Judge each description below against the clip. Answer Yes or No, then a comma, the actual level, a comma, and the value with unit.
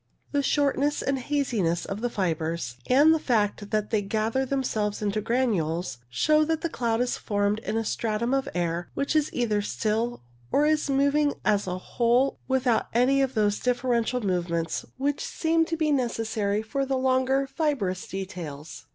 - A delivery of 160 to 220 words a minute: Yes, average, 170 wpm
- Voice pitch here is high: Yes, high, 235 Hz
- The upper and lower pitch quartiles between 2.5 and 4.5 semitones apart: No, average, 5.1 semitones